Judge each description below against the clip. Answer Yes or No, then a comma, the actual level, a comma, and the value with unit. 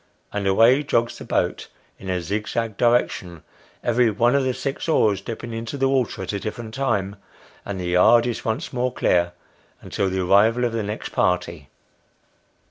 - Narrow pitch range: No, average, 3.8 semitones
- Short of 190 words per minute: Yes, average, 175 wpm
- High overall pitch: No, low, 110 Hz